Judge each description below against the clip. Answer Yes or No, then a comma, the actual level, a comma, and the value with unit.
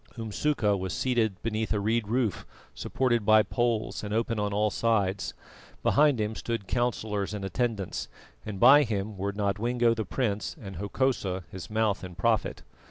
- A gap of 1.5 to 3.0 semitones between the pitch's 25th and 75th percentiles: Yes, narrow, 2.6 semitones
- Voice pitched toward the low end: Yes, low, 110 Hz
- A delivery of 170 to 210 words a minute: No, average, 160 wpm